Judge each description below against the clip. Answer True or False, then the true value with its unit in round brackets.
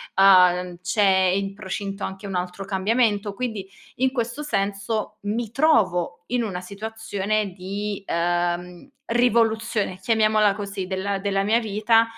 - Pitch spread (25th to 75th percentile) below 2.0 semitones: False (2.7 semitones)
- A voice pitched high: True (200 Hz)